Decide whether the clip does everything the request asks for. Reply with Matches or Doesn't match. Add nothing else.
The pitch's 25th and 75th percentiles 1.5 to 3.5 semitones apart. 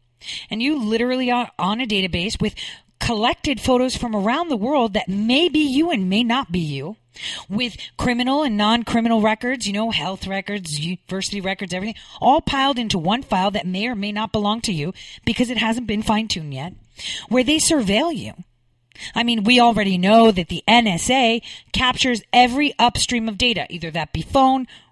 Doesn't match